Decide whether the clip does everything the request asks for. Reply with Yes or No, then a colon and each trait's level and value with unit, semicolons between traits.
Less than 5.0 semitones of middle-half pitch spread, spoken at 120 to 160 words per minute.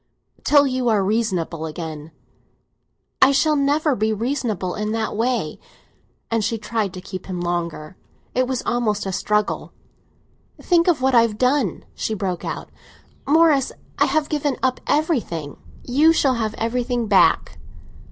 No: wide, 5.5 semitones; average, 150 wpm